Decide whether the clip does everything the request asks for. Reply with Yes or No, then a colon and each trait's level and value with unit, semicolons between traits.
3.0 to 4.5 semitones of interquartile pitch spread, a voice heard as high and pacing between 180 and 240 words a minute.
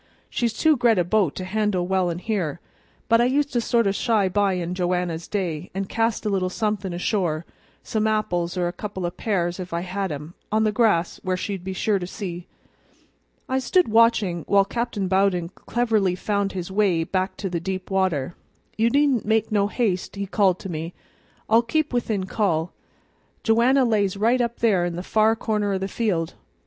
Yes: average, 3.7 semitones; high, 195 Hz; average, 195 wpm